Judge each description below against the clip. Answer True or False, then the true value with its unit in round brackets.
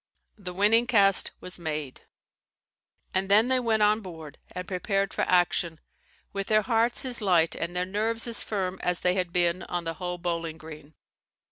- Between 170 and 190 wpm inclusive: True (175 wpm)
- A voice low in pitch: False (185 Hz)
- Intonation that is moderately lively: True (3.7 semitones)